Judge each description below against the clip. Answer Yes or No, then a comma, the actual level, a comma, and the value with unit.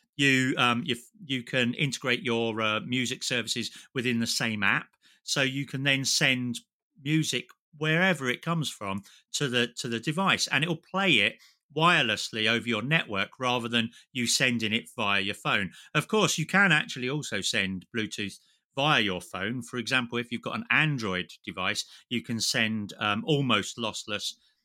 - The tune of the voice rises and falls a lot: No, average, 4.1 semitones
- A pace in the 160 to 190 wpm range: Yes, average, 175 wpm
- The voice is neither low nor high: No, low, 125 Hz